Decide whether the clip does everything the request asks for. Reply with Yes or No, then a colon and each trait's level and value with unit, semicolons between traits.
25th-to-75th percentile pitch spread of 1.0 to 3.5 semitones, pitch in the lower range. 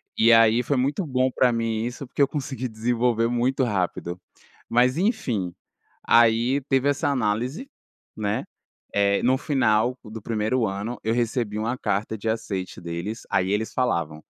Yes: average, 3.1 semitones; low, 115 Hz